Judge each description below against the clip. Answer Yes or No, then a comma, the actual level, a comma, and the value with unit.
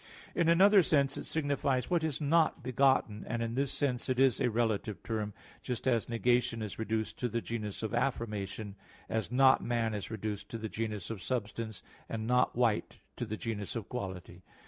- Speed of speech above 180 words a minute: Yes, average, 190 wpm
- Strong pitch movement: No, average, 3.3 semitones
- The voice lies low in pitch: Yes, low, 115 Hz